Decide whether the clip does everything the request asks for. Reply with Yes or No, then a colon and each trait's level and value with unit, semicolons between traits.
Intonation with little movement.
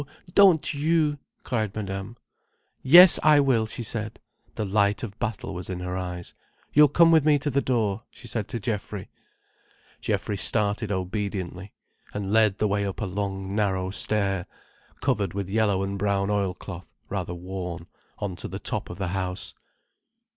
No: average, 3.0 semitones